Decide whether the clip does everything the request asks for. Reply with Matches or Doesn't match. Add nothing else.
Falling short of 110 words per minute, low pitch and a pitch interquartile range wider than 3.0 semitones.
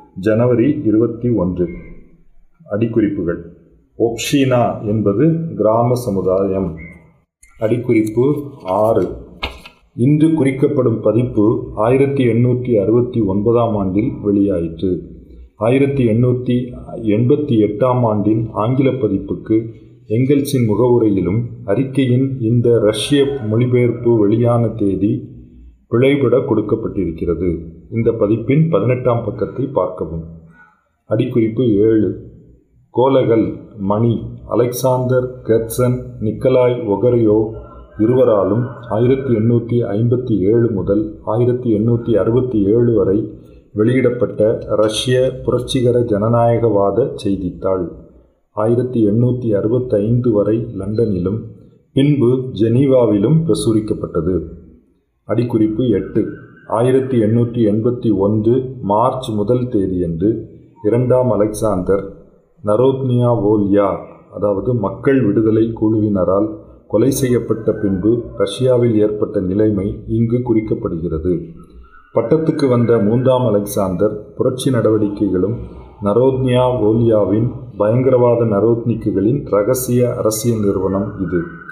Matches